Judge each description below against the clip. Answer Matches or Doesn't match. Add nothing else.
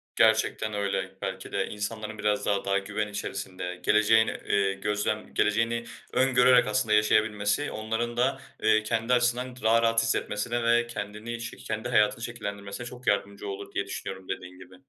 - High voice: Doesn't match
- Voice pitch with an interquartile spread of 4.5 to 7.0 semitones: Doesn't match